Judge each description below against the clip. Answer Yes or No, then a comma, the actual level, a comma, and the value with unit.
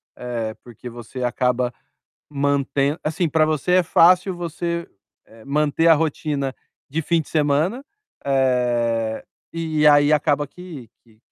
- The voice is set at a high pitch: No, medium, 145 Hz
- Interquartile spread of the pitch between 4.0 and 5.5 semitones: Yes, average, 4.5 semitones